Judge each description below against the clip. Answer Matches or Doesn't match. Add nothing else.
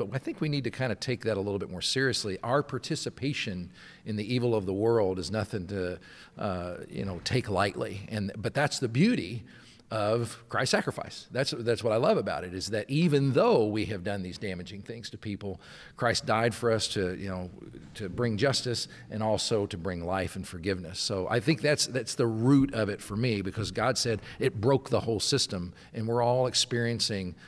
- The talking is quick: Matches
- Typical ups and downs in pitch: Matches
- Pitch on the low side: Matches